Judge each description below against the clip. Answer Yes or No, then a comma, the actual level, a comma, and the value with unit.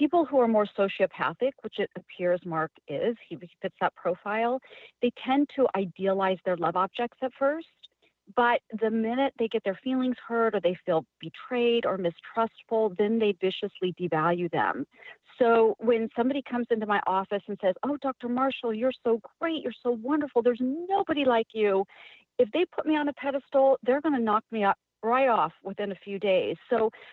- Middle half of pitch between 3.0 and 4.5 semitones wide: No, average, 4.9 semitones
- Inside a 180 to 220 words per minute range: Yes, average, 190 wpm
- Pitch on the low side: No, high, 230 Hz